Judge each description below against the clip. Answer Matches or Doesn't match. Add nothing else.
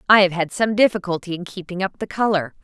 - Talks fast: Matches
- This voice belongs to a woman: Matches